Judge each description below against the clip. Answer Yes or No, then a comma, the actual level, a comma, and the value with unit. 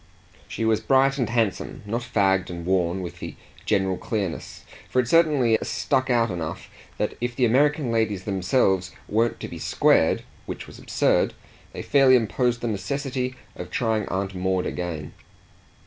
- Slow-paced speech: No, average, 160 wpm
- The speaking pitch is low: Yes, low, 110 Hz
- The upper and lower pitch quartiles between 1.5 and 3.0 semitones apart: No, average, 5.0 semitones